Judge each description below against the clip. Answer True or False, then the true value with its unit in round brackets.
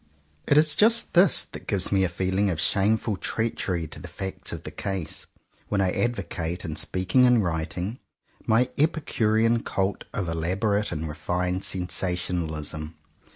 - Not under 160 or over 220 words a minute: False (150 wpm)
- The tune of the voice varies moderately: True (4.2 semitones)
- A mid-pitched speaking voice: False (95 Hz)